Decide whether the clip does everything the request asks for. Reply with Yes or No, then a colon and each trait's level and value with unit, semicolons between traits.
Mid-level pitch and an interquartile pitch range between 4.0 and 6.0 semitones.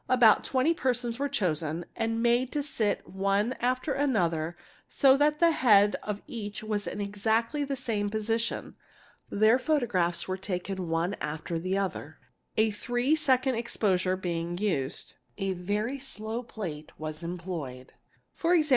No: high, 210 Hz; wide, 5.6 semitones